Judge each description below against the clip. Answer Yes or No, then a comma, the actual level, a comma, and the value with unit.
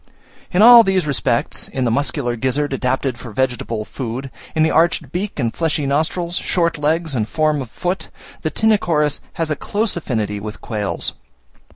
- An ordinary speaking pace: Yes, average, 170 wpm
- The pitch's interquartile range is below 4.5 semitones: No, wide, 5.4 semitones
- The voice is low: No, medium, 145 Hz